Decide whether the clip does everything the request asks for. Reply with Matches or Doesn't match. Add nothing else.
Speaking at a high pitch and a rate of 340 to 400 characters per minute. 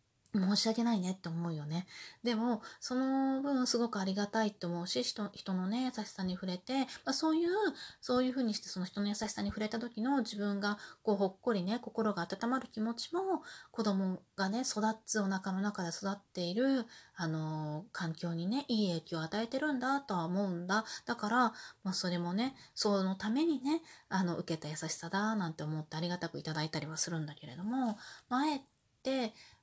Matches